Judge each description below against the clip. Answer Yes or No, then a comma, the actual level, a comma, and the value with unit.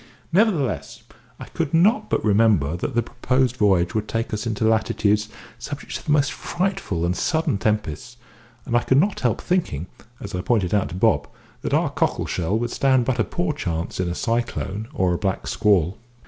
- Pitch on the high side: No, low, 110 Hz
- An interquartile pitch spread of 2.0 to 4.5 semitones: No, wide, 5.5 semitones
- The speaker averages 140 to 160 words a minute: No, average, 190 wpm